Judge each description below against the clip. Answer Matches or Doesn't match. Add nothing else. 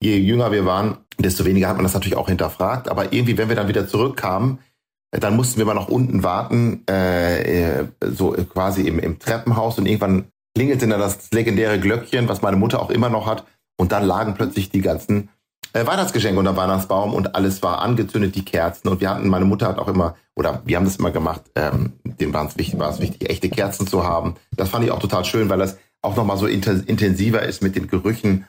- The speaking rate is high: Matches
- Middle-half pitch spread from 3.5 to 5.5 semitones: Doesn't match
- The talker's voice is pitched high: Doesn't match